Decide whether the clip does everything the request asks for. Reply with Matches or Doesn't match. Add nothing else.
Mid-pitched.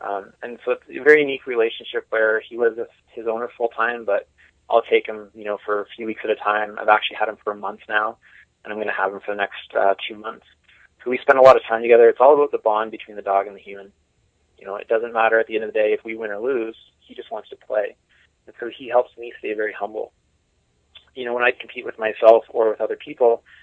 Doesn't match